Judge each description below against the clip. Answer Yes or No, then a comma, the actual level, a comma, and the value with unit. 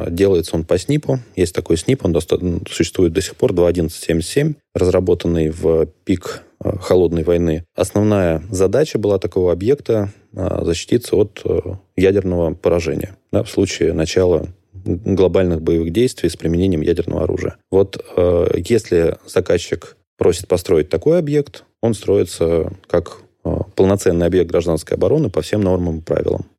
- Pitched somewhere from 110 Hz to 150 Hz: No, very low, 90 Hz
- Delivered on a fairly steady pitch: No, average, 3.4 semitones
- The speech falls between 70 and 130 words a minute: No, average, 140 wpm